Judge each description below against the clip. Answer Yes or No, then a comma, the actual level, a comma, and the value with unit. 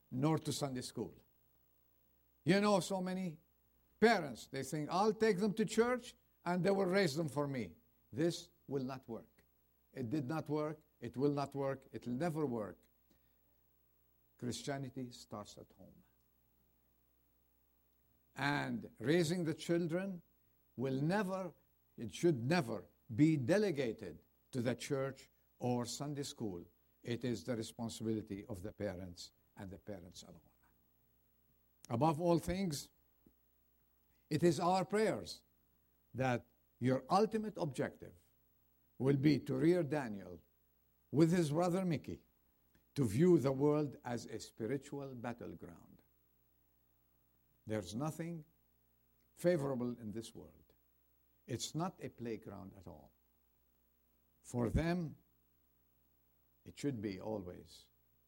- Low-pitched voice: Yes, low, 110 Hz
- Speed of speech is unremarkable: No, slow, 120 wpm